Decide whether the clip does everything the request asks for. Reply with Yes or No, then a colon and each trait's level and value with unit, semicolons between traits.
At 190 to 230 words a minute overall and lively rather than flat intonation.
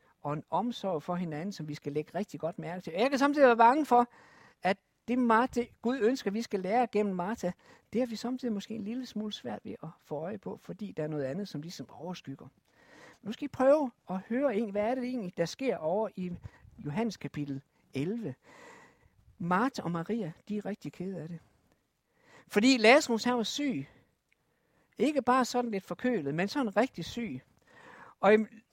Yes: average, 195 wpm; wide, 5.7 semitones